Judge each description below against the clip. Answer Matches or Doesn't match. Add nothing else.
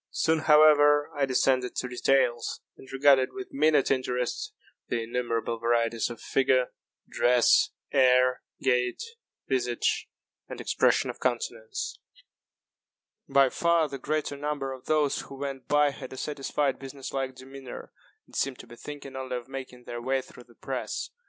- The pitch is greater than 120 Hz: Matches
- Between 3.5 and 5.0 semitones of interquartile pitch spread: Doesn't match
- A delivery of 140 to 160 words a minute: Matches